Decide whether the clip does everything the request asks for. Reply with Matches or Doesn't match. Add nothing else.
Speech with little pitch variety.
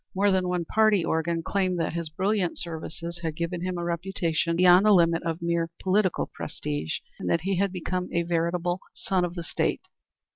Matches